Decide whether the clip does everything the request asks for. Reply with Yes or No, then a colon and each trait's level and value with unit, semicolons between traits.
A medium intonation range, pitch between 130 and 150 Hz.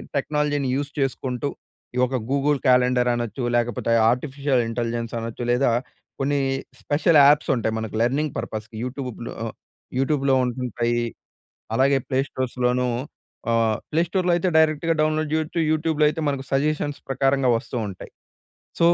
Yes: average, 3.2 semitones; low, 135 Hz